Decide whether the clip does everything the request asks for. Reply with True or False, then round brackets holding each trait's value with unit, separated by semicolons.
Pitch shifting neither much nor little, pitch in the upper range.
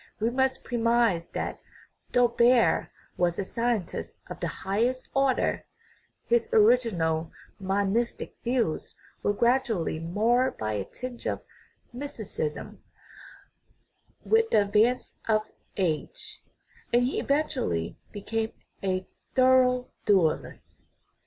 True (4.9 semitones; 230 Hz)